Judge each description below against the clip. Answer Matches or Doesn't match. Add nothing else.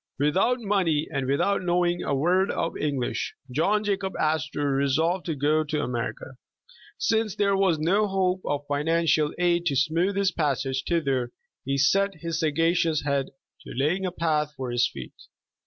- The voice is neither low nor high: Matches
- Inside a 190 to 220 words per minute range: Doesn't match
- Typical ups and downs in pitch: Matches